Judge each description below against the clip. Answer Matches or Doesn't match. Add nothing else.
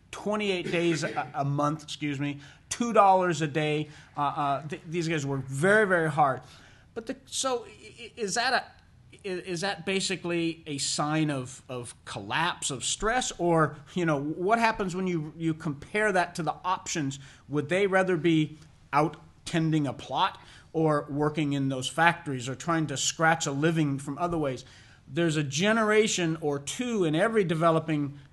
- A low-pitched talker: Doesn't match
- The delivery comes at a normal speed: Matches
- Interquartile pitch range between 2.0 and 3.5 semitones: Doesn't match